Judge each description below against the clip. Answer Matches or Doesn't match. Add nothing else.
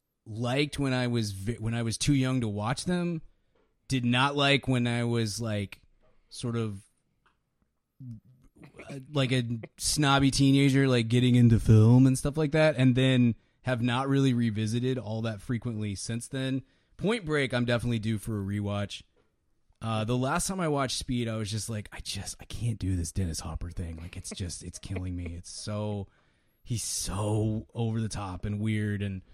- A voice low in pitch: Matches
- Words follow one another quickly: Doesn't match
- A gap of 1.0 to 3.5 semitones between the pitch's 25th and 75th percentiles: Doesn't match